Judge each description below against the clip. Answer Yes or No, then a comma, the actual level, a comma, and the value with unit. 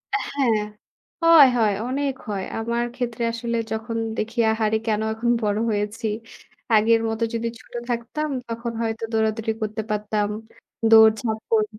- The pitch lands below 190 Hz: No, high, 225 Hz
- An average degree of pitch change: No, narrow, 1.5 semitones